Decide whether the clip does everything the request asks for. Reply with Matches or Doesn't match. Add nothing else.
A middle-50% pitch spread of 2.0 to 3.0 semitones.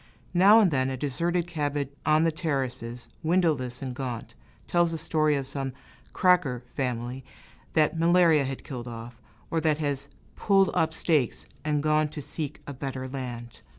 Doesn't match